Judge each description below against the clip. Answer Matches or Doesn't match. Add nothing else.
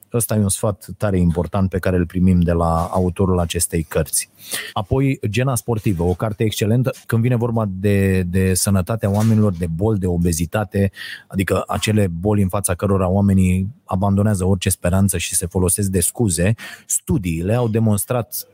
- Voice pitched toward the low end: Matches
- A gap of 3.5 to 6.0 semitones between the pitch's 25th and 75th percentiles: Doesn't match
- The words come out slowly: Doesn't match